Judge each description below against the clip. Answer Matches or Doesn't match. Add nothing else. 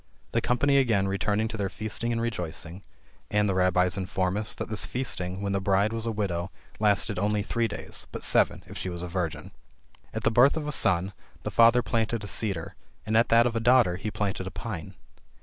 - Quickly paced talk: Matches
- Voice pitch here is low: Matches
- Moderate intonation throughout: Matches